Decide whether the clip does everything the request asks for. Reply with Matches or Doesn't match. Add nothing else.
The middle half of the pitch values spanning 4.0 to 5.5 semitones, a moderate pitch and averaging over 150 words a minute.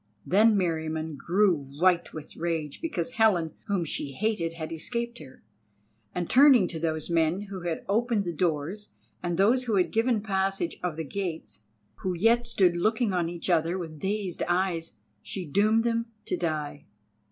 Matches